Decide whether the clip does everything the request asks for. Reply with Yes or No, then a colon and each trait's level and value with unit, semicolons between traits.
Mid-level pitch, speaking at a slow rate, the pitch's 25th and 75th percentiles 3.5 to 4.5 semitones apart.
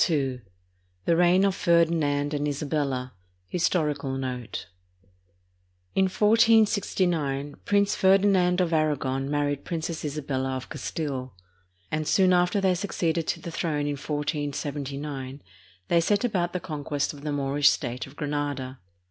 Yes: medium, 150 Hz; slow, 130 wpm; average, 4.0 semitones